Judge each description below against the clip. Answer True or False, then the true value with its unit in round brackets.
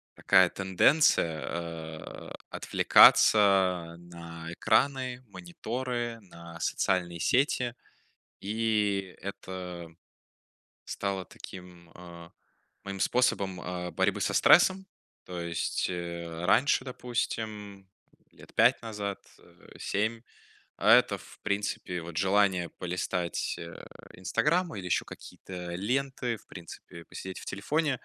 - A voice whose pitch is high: False (95 Hz)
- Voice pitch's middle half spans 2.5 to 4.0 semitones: False (4.7 semitones)